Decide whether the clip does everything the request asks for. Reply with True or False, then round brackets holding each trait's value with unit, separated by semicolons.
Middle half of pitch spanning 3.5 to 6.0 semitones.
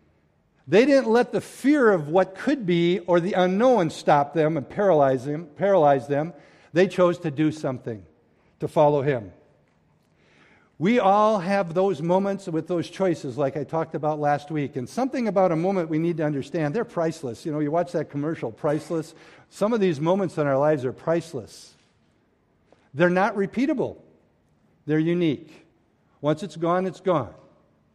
True (4.4 semitones)